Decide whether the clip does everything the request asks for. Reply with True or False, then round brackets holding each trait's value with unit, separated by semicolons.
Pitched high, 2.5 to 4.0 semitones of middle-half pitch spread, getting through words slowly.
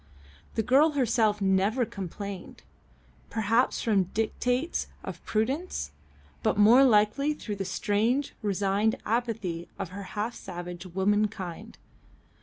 True (210 Hz; 3.6 semitones; 105 wpm)